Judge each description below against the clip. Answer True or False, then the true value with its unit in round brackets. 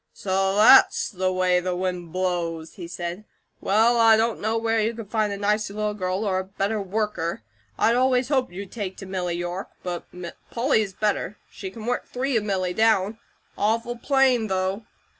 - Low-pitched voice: False (205 Hz)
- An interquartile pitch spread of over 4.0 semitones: False (3.3 semitones)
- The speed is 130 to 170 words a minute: False (185 wpm)